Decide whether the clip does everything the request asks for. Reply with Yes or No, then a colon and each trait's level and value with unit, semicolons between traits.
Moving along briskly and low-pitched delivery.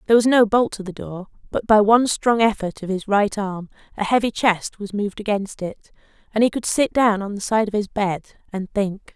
No: fast, 235 wpm; high, 210 Hz